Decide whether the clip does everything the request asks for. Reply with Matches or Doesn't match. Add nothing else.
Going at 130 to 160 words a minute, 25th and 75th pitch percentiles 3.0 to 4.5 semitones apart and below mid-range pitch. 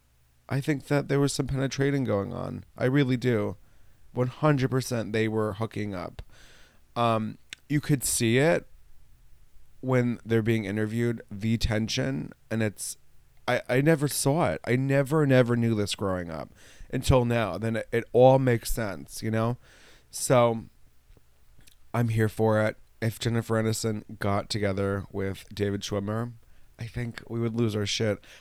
Matches